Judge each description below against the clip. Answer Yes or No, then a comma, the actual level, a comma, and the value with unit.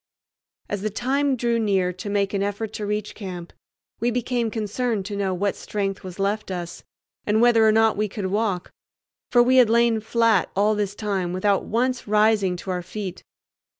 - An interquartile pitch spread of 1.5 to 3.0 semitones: Yes, average, 2.7 semitones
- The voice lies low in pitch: No, high, 210 Hz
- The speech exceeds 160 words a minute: Yes, average, 185 wpm